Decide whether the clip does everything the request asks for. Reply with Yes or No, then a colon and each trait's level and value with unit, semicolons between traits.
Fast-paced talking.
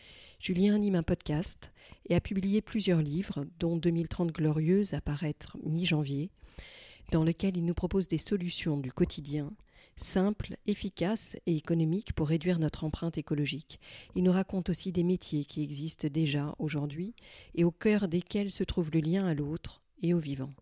No: average, 165 wpm